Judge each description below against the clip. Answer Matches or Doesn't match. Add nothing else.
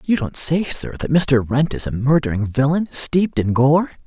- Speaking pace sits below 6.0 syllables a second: Matches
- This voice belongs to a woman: Doesn't match